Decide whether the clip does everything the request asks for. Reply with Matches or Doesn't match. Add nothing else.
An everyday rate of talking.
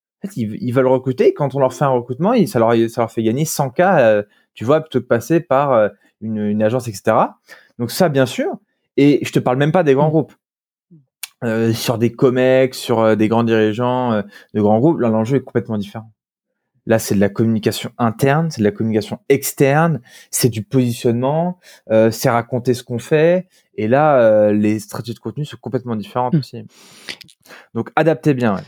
Matches